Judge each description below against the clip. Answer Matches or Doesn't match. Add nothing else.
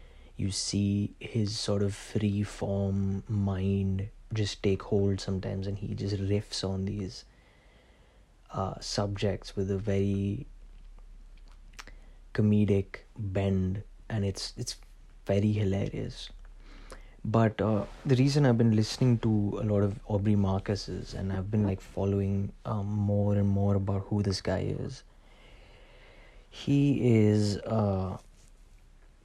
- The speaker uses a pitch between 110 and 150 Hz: Doesn't match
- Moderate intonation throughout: Doesn't match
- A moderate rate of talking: Doesn't match